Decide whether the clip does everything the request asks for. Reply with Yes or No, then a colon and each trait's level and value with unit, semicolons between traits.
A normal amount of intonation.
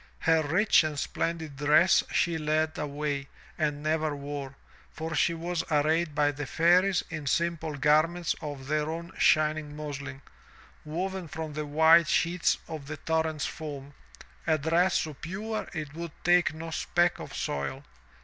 No: narrow, 2.3 semitones